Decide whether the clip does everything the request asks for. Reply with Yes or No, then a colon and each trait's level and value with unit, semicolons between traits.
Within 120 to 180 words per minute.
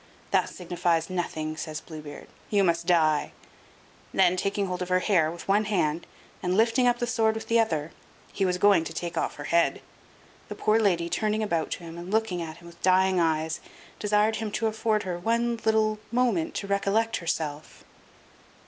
No: average, 190 wpm